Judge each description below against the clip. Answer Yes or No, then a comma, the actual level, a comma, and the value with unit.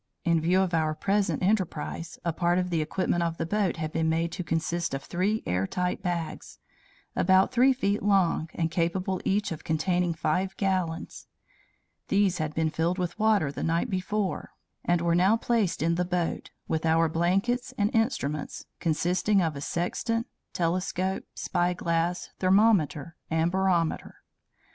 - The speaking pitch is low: No, medium, 175 Hz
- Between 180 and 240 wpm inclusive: No, average, 155 wpm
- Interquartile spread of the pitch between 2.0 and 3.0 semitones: Yes, average, 2.7 semitones